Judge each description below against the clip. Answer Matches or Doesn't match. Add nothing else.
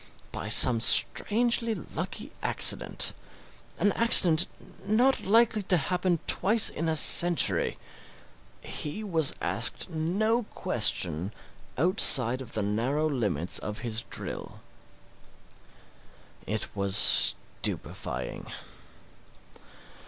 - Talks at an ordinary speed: Doesn't match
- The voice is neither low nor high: Matches